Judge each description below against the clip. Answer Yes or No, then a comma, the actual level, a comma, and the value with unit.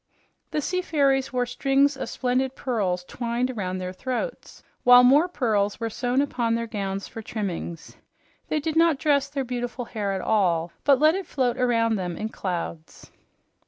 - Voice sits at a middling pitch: No, high, 245 Hz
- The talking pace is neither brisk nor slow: Yes, average, 170 wpm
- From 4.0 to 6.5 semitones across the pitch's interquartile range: Yes, average, 5.0 semitones